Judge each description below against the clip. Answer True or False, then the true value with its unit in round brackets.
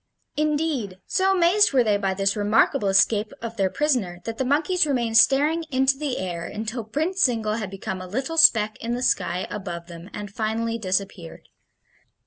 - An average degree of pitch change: False (6.0 semitones)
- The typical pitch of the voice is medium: False (225 Hz)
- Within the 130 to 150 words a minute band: False (175 wpm)